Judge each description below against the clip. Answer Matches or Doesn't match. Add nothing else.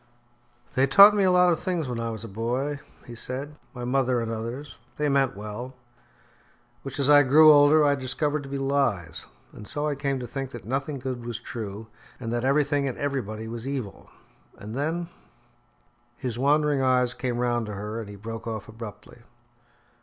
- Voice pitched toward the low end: Matches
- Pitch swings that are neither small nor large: Matches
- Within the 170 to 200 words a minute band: Matches